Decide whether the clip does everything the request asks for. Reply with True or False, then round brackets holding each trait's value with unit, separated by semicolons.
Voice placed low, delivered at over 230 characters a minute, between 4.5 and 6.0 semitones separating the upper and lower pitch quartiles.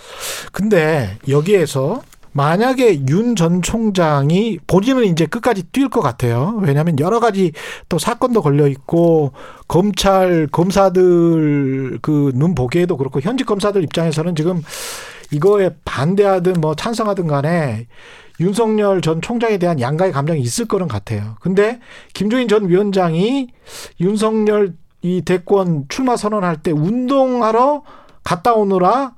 False (180 Hz; 280 characters per minute; 5.4 semitones)